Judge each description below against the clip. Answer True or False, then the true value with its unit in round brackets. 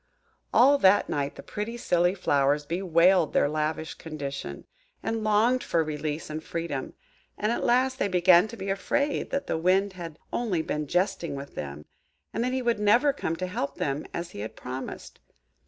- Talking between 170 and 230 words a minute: True (180 wpm)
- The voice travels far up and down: True (5.7 semitones)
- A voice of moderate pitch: True (175 Hz)